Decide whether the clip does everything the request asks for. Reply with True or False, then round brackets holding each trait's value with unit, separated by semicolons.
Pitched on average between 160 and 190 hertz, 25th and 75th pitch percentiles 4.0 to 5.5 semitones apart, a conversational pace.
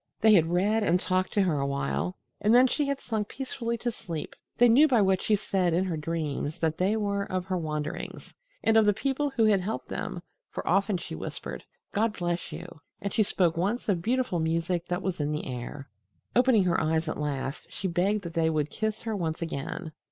False (185 Hz; 5.0 semitones; 220 wpm)